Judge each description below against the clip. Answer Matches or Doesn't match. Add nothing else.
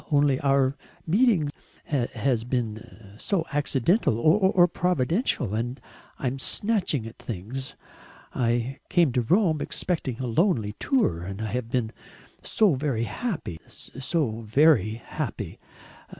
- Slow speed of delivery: Matches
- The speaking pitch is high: Doesn't match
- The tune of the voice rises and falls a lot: Matches